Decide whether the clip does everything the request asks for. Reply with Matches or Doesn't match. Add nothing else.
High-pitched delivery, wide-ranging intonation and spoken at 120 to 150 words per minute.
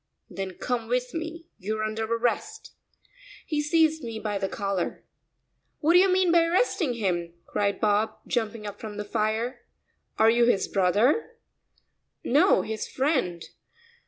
Matches